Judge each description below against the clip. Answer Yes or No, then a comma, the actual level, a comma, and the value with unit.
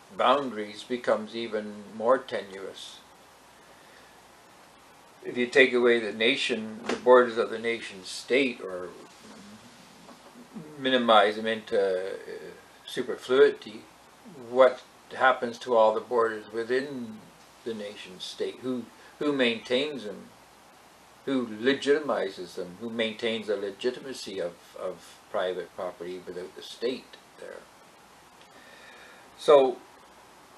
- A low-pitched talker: Yes, low, 120 Hz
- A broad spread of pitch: No, average, 3.2 semitones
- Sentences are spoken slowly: Yes, slow, 100 wpm